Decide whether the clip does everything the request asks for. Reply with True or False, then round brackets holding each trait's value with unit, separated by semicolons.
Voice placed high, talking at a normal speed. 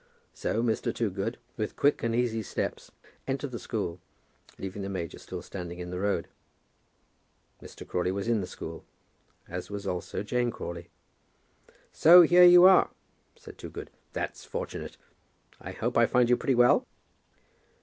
False (110 Hz; 150 wpm)